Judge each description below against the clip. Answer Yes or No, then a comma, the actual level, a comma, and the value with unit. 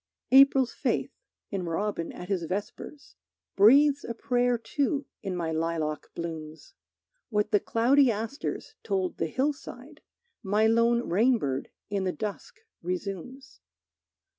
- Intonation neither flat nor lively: No, wide, 6.3 semitones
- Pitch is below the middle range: No, high, 210 Hz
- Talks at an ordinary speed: No, slow, 120 wpm